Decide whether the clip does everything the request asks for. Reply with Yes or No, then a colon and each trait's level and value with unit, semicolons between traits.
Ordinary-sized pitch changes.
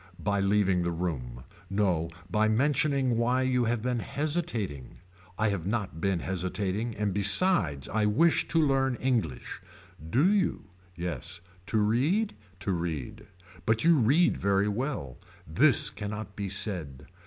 No: wide, 5.7 semitones